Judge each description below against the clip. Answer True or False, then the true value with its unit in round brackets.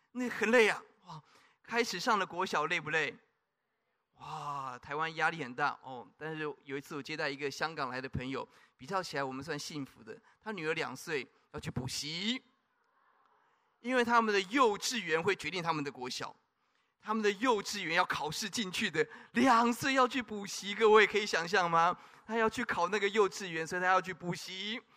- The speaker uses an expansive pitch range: True (6.4 semitones)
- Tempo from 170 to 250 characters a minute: False (275 characters per minute)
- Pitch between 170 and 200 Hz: True (190 Hz)